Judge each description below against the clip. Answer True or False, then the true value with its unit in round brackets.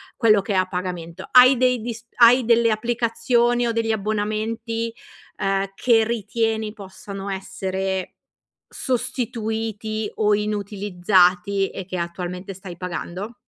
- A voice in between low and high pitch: False (215 Hz)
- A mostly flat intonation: False (3.1 semitones)